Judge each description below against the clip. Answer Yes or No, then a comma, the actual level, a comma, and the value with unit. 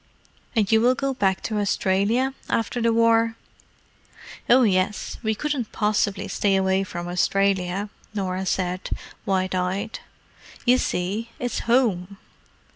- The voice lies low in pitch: No, high, 205 Hz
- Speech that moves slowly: Yes, slow, 125 wpm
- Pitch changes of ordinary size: Yes, average, 3.3 semitones